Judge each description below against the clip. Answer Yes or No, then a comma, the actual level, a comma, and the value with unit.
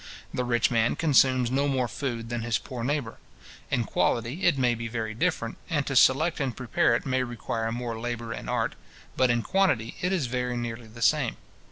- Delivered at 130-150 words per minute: No, average, 200 wpm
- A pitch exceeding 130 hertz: No, low, 120 Hz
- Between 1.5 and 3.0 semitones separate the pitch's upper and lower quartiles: Yes, narrow, 2.5 semitones